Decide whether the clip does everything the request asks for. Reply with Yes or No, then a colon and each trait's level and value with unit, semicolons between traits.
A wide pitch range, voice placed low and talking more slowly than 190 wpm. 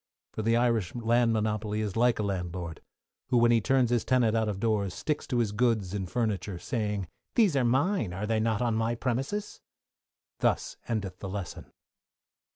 No: average, 2.9 semitones; low, 110 Hz; average, 180 wpm